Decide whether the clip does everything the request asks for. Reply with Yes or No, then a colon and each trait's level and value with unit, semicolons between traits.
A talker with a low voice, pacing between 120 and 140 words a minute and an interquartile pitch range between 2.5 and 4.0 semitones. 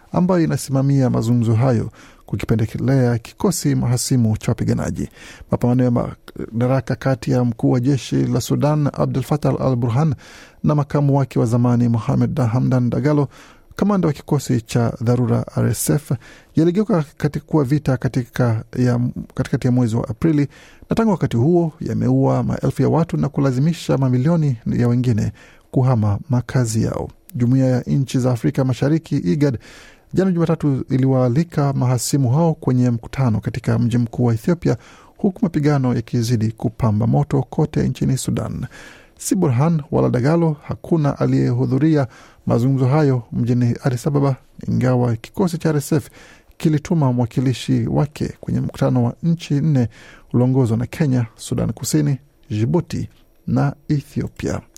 Yes: low, 130 Hz; average, 130 wpm; average, 3.5 semitones